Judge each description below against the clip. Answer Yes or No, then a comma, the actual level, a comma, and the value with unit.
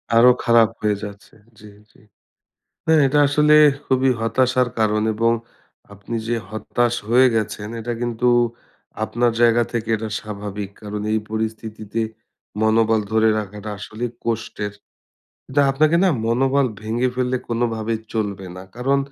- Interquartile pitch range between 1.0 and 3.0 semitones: Yes, narrow, 2.5 semitones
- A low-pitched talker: Yes, low, 115 Hz